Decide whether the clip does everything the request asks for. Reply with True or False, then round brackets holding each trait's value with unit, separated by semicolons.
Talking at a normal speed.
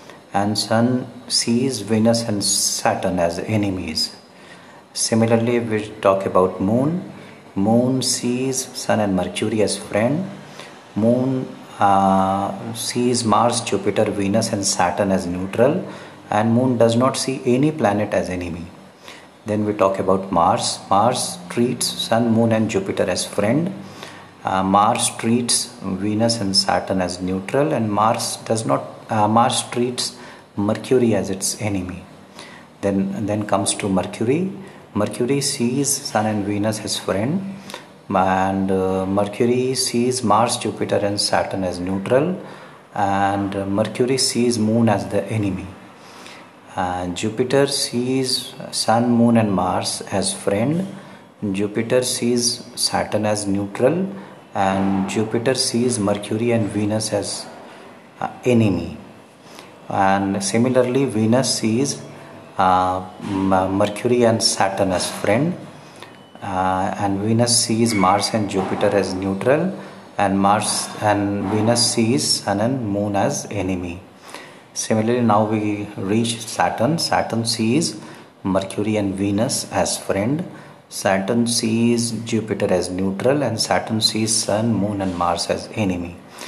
False (125 wpm)